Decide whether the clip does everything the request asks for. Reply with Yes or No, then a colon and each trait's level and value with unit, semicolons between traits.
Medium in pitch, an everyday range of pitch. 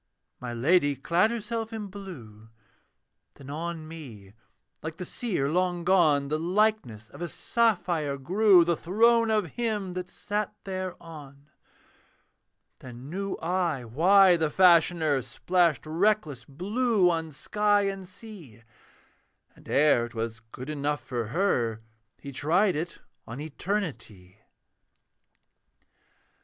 No: medium, 170 Hz; wide, 5.9 semitones